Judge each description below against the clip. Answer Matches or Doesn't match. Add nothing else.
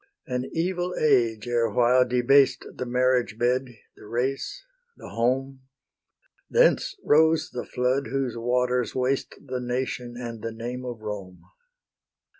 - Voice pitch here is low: Matches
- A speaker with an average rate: Doesn't match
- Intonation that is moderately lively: Doesn't match